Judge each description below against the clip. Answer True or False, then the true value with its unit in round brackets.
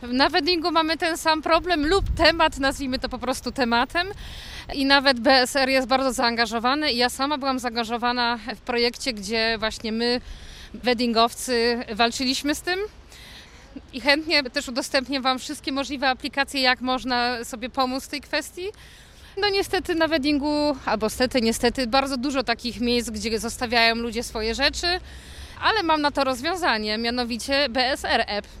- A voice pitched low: False (265 Hz)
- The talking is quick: False (150 wpm)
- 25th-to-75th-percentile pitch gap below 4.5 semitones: True (3.6 semitones)